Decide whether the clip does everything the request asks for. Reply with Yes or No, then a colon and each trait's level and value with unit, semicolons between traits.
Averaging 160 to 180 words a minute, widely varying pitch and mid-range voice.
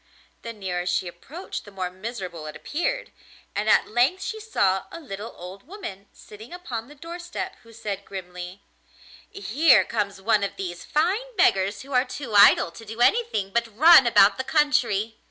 No: average, 175 wpm; wide, 7.5 semitones; high, 225 Hz